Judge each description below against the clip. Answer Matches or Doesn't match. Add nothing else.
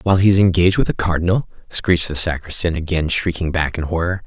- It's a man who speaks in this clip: Matches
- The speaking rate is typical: Doesn't match